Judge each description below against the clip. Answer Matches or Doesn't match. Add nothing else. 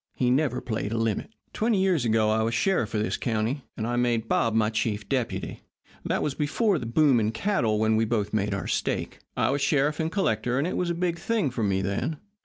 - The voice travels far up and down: Matches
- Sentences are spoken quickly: Matches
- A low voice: Matches